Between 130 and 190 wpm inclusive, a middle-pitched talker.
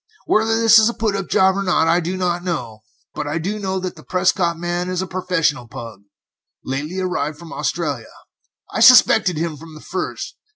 No: average, 200 wpm; medium, 175 Hz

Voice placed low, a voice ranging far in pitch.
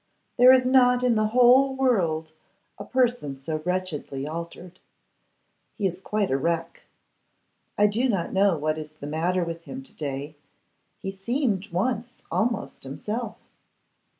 No: high, 195 Hz; wide, 7.3 semitones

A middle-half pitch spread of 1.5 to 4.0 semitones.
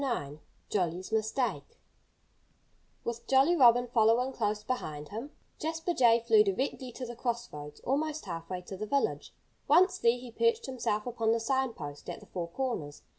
No: average, 4.7 semitones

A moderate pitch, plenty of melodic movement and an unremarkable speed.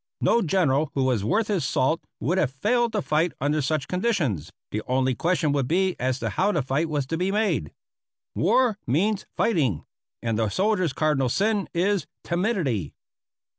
Yes: medium, 160 Hz; wide, 6.9 semitones; average, 170 wpm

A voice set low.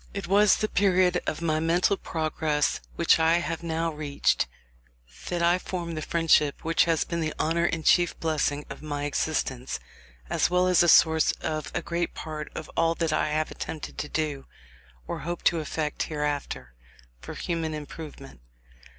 No: medium, 160 Hz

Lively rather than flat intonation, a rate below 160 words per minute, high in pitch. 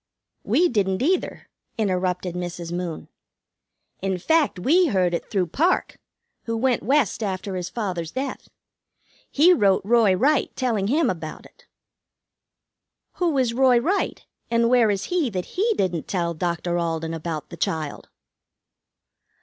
Yes: wide, 6.8 semitones; average, 140 wpm; high, 195 Hz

